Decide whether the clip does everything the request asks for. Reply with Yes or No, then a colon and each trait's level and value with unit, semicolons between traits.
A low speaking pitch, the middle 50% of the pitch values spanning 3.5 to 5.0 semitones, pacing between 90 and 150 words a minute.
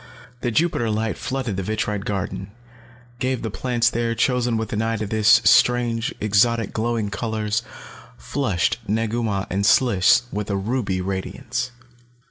No: low, 110 Hz; average, 2.9 semitones; average, 145 wpm